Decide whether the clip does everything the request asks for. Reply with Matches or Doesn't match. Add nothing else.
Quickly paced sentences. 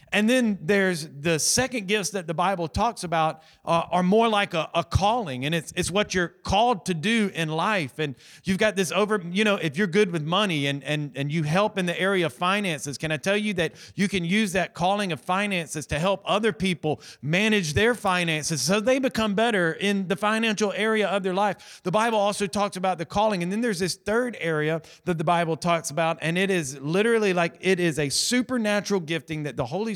Matches